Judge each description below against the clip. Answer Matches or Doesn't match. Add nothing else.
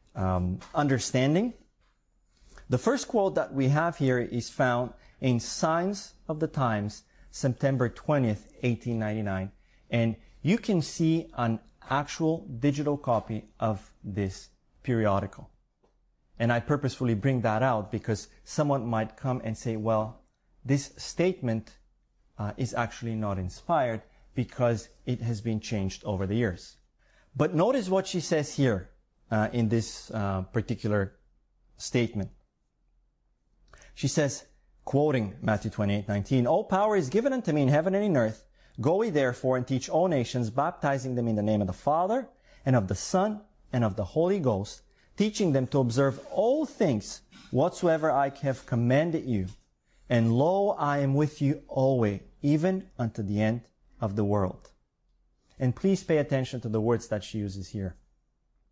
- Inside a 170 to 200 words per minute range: Doesn't match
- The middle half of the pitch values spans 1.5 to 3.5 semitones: Doesn't match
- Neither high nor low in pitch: Doesn't match